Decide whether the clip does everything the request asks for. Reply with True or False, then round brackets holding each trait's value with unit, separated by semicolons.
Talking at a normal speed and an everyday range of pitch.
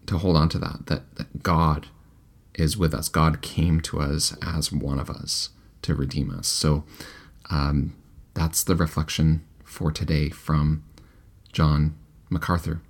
False (150 wpm; 1.5 semitones)